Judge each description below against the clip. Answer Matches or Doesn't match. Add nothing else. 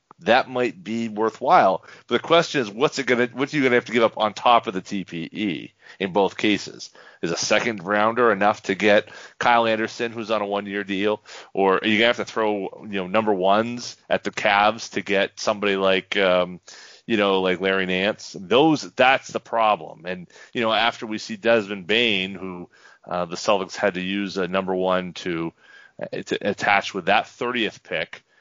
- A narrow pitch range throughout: Doesn't match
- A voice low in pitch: Matches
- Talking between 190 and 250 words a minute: Matches